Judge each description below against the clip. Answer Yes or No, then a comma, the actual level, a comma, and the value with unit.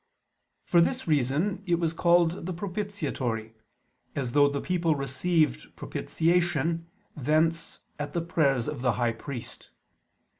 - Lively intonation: No, average, 3.9 semitones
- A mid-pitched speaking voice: Yes, medium, 160 Hz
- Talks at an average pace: No, slow, 125 wpm